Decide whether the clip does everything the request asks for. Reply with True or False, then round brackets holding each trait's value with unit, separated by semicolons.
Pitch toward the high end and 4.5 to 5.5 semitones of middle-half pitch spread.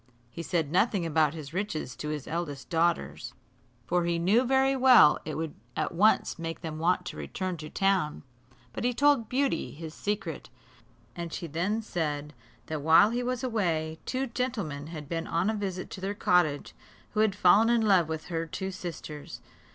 False (175 Hz; 5.1 semitones)